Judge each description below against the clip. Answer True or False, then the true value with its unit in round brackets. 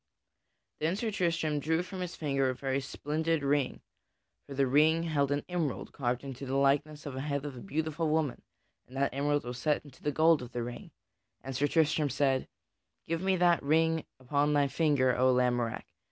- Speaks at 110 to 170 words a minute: False (195 wpm)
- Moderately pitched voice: True (145 Hz)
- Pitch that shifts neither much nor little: True (3.1 semitones)